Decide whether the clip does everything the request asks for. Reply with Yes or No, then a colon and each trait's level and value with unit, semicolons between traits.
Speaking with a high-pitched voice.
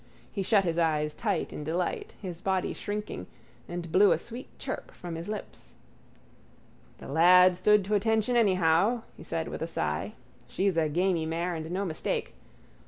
No: medium, 180 Hz